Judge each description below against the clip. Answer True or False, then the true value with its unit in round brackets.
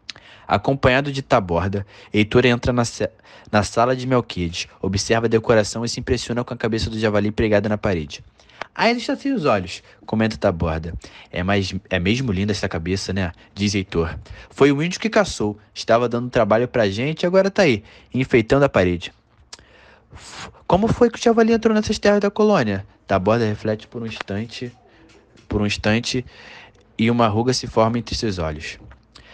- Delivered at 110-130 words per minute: False (175 wpm)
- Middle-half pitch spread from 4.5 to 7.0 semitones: False (4.1 semitones)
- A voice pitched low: True (110 Hz)